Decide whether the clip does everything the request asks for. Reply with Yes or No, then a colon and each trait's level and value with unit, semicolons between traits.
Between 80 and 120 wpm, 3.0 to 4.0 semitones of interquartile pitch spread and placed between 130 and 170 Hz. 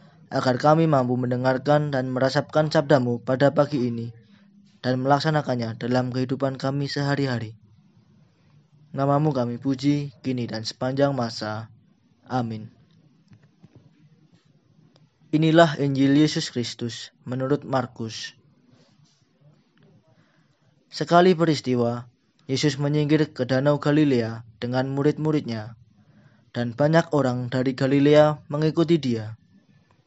Yes: average, 90 wpm; average, 3.4 semitones; low, 135 Hz